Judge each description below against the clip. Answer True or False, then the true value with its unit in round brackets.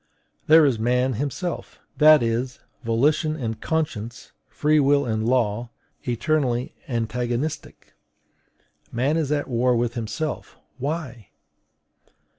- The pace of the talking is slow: True (105 wpm)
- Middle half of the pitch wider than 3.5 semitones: True (4.3 semitones)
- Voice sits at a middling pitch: False (125 Hz)